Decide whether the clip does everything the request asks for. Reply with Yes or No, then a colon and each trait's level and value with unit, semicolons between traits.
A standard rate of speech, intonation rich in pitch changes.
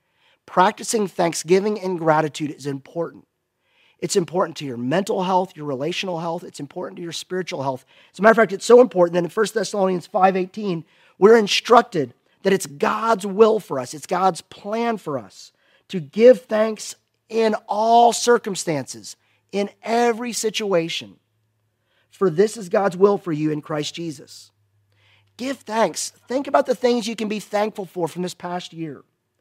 Yes: average, 165 wpm; wide, 6.3 semitones